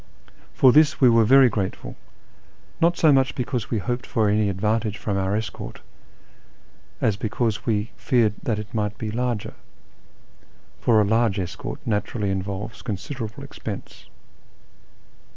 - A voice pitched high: No, low, 110 Hz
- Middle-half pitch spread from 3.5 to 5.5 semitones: No, average, 3.0 semitones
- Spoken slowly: No, average, 145 wpm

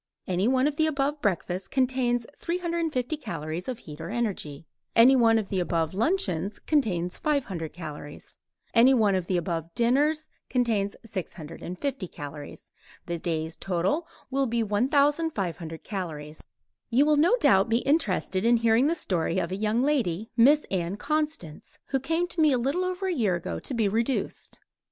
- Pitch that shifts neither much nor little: No, wide, 7.8 semitones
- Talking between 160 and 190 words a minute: Yes, average, 165 wpm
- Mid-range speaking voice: No, high, 225 Hz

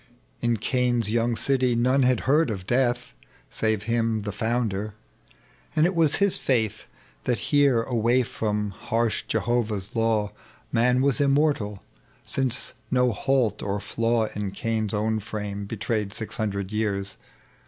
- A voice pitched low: Yes, low, 115 Hz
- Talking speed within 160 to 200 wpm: No, average, 140 wpm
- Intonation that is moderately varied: Yes, average, 3.1 semitones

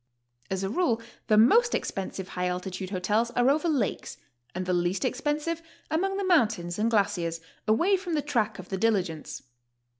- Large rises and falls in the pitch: Yes, wide, 8.3 semitones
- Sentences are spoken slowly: No, average, 170 wpm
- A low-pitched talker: No, high, 220 Hz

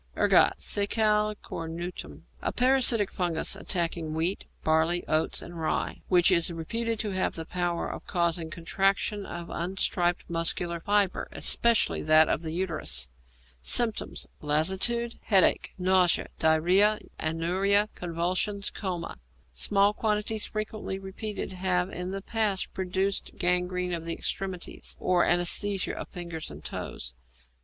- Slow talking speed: Yes, slow, 125 wpm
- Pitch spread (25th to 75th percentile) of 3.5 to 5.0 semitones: No, average, 3.1 semitones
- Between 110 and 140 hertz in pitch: No, medium, 180 Hz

